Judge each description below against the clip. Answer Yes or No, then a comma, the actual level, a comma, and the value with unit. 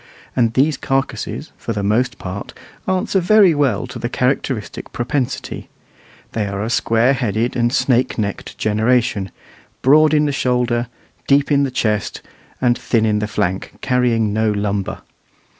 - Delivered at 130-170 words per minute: Yes, average, 145 wpm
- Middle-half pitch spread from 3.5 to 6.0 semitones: Yes, average, 4.0 semitones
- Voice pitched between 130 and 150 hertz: No, low, 120 Hz